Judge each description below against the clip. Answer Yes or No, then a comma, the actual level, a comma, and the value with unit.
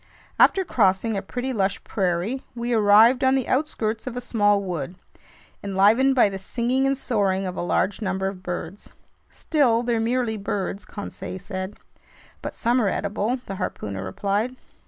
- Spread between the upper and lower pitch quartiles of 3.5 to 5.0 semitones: Yes, average, 4.3 semitones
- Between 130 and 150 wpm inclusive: No, average, 160 wpm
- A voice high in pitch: Yes, high, 210 Hz